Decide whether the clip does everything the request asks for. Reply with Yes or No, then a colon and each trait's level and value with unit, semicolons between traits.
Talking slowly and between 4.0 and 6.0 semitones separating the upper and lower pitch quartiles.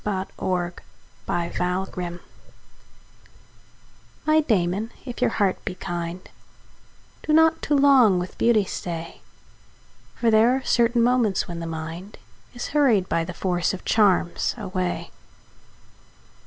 Yes: slow, 130 wpm; average, 5.1 semitones